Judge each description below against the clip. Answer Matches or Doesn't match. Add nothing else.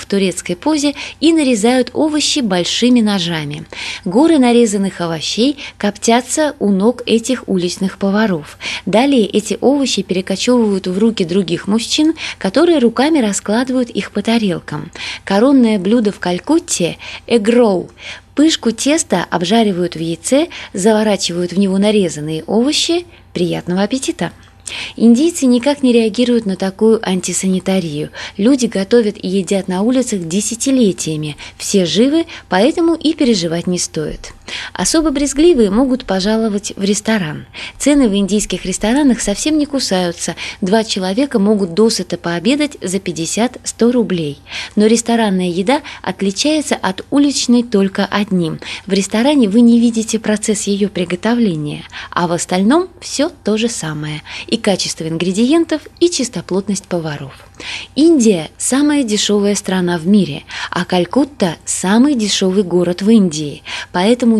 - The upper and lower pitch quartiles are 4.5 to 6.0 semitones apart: Matches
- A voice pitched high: Matches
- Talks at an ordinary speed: Matches